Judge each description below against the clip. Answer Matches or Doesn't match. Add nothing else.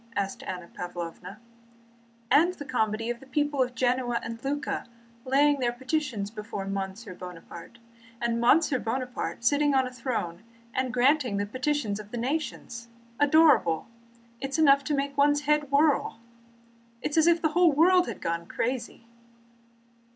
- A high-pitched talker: Matches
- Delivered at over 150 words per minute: Matches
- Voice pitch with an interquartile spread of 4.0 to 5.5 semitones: Matches